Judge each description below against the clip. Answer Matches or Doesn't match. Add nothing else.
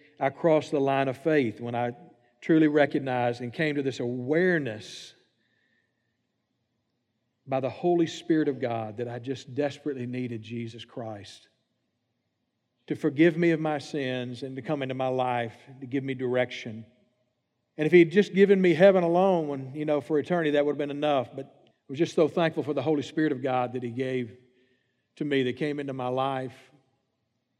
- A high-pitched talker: Doesn't match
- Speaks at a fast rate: Doesn't match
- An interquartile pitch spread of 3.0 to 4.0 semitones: Matches